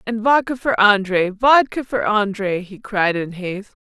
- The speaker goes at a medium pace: Yes, average, 170 wpm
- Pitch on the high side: Yes, high, 210 Hz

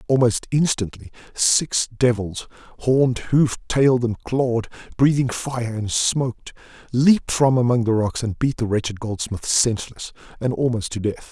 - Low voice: Yes, low, 120 Hz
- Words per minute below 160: Yes, average, 150 wpm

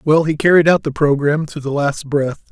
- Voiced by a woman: No, male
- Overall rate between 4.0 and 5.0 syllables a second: No, 5.5 syllables/s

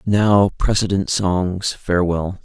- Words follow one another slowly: Yes, slow, 100 wpm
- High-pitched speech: No, very low, 95 Hz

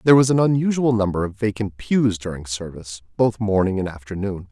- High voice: No, low, 105 Hz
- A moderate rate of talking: Yes, average, 185 wpm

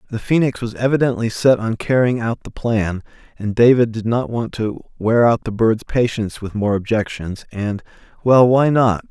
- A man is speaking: Yes, male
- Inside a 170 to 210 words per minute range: Yes, average, 180 wpm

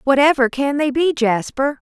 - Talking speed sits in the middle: Yes, average, 155 wpm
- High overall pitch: Yes, very high, 275 Hz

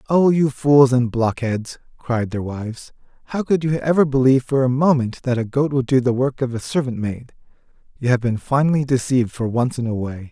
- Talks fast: Yes, fast, 215 wpm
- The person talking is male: Yes, male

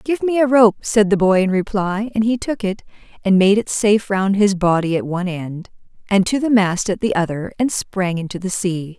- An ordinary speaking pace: No, fast, 235 wpm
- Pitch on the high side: Yes, high, 200 Hz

